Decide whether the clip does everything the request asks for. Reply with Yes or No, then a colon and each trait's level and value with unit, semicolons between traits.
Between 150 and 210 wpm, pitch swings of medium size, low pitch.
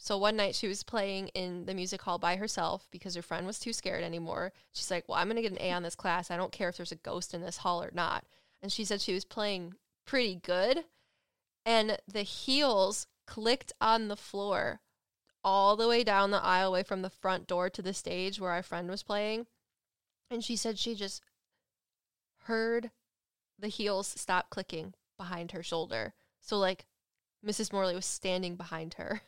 No: average, 200 wpm; average, 3.0 semitones; high, 195 Hz